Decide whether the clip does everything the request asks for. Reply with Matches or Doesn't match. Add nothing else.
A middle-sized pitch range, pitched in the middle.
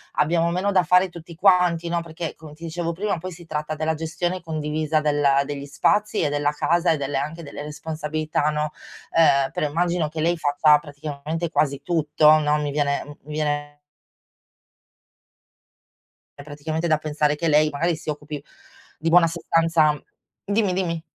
Doesn't match